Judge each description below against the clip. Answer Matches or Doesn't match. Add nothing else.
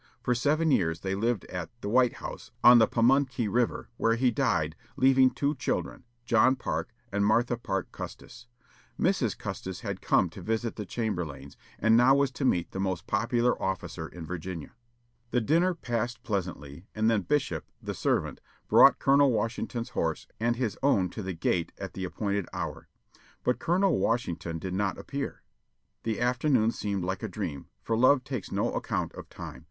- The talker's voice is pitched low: Matches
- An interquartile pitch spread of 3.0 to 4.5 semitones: Doesn't match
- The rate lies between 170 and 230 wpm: Matches